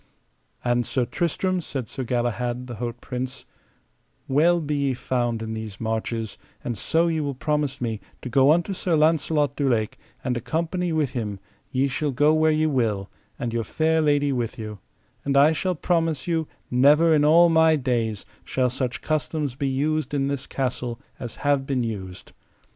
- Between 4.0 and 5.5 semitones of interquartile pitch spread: Yes, average, 4.4 semitones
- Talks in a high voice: No, low, 135 Hz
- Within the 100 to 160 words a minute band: No, average, 175 wpm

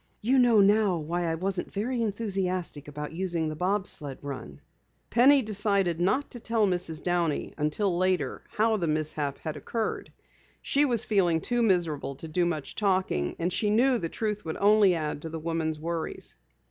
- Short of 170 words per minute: No, average, 175 wpm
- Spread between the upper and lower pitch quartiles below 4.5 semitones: No, average, 4.9 semitones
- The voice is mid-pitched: Yes, medium, 180 Hz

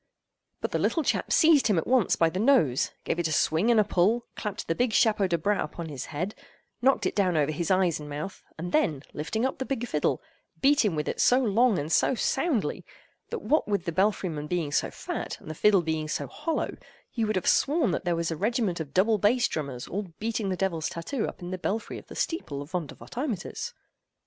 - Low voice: No, high, 190 Hz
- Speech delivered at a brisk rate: Yes, fast, 230 wpm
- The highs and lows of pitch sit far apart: Yes, wide, 6.3 semitones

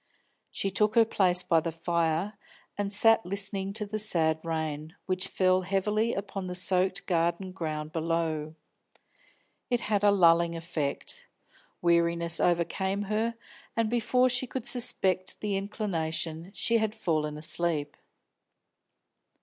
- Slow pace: Yes, slow, 130 wpm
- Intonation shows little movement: No, average, 3.8 semitones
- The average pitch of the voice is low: No, medium, 185 Hz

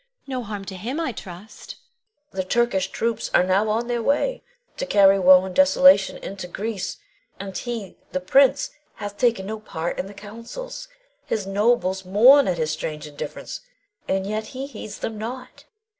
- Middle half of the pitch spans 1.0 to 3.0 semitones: No, average, 4.1 semitones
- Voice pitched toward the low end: No, high, 210 Hz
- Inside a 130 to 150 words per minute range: No, average, 175 wpm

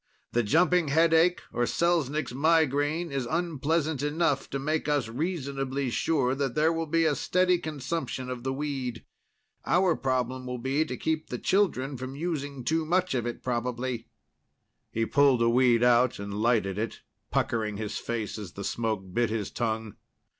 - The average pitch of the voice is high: No, low, 135 Hz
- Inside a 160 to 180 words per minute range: Yes, average, 165 wpm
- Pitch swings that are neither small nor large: Yes, average, 4.8 semitones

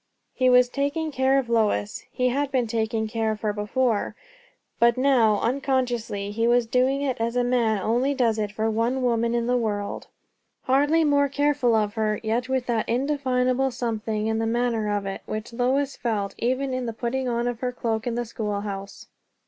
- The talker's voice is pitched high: Yes, high, 240 Hz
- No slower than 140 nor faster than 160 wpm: No, average, 190 wpm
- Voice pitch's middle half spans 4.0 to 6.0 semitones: No, average, 2.8 semitones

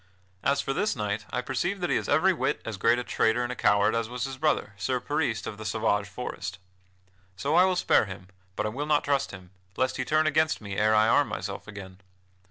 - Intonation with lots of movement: Yes, wide, 5.7 semitones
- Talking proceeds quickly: Yes, fast, 235 wpm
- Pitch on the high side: No, low, 120 Hz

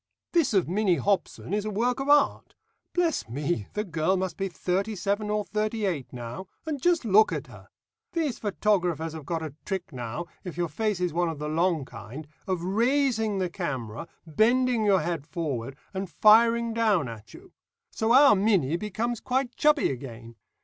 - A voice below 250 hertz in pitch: Yes, high, 190 Hz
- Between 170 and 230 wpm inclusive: Yes, average, 180 wpm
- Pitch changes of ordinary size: No, wide, 5.8 semitones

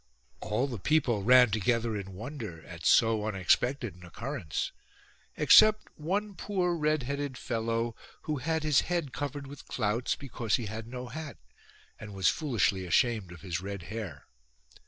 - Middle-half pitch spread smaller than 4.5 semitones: No, wide, 5.6 semitones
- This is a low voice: Yes, low, 120 Hz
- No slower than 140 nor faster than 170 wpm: Yes, average, 155 wpm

